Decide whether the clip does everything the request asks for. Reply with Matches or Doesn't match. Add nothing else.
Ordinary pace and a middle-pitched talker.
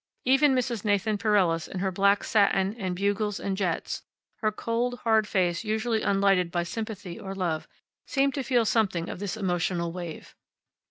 Doesn't match